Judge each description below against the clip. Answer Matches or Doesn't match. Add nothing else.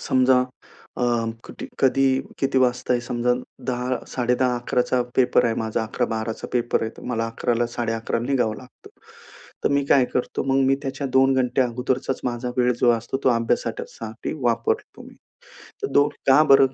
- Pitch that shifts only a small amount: Matches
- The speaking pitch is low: Matches